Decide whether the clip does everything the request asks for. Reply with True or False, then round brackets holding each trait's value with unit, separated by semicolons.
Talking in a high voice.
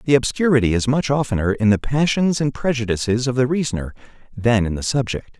False (125 Hz)